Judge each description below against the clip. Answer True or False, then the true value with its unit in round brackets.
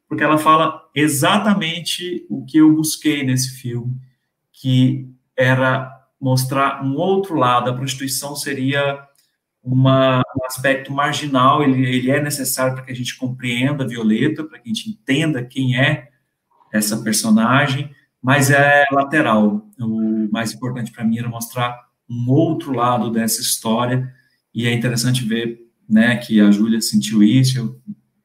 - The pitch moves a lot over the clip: False (2.9 semitones)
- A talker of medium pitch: False (130 Hz)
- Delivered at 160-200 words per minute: False (145 wpm)